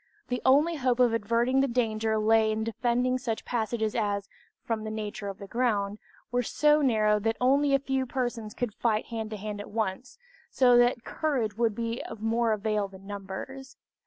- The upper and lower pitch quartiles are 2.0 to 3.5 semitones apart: Yes, average, 2.7 semitones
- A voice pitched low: No, high, 230 Hz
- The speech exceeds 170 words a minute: Yes, average, 190 wpm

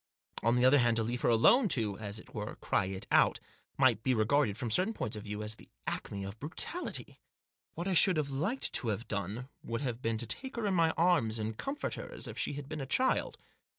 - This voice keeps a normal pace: No, fast, 240 wpm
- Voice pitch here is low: Yes, low, 120 Hz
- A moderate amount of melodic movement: No, wide, 6.5 semitones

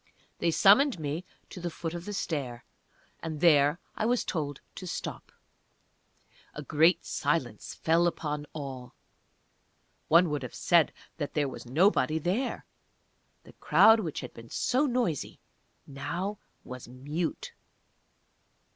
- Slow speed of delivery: Yes, slow, 130 wpm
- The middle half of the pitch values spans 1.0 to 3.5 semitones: No, average, 4.2 semitones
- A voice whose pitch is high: No, medium, 160 Hz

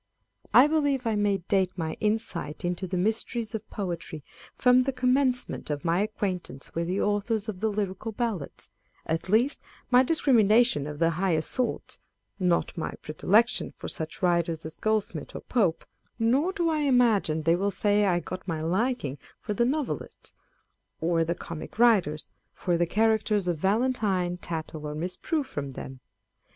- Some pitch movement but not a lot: No, wide, 5.7 semitones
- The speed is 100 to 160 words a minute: No, average, 170 wpm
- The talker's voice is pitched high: Yes, high, 195 Hz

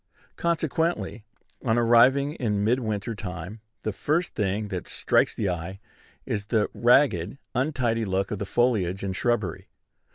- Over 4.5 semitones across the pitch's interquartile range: No, average, 4.1 semitones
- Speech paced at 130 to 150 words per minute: Yes, average, 140 wpm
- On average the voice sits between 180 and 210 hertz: No, low, 110 Hz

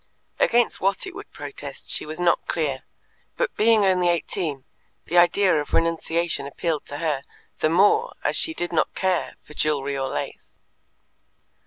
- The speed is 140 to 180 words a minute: Yes, average, 160 wpm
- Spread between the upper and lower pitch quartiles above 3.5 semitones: Yes, average, 4.3 semitones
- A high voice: No, medium, 170 Hz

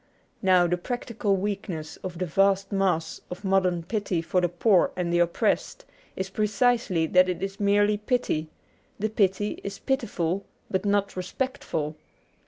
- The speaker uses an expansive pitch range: No, average, 2.7 semitones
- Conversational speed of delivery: Yes, average, 150 wpm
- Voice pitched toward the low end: No, high, 190 Hz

